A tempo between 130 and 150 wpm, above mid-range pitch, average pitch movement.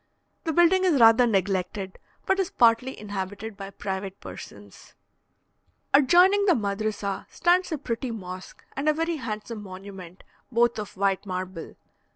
No: average, 140 wpm; high, 215 Hz; wide, 6.7 semitones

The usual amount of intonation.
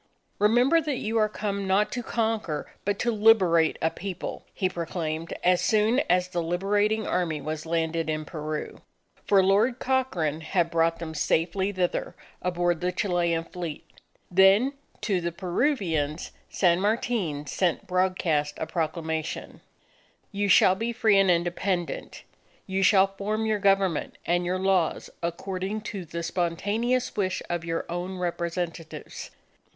Yes: average, 3.4 semitones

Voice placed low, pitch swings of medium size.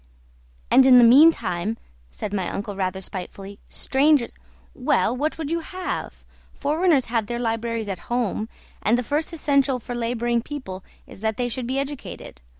No: high, 240 Hz; average, 4.8 semitones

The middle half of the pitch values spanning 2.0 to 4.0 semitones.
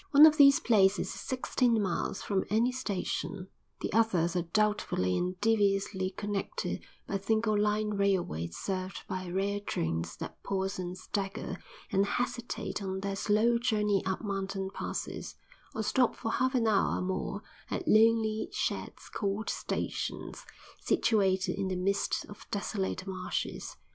Yes: narrow, 2.6 semitones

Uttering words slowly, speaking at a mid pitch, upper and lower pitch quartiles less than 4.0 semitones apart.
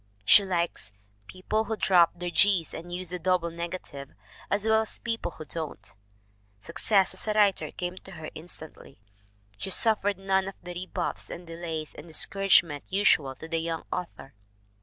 No: average, 175 wpm; medium, 175 Hz; average, 2.9 semitones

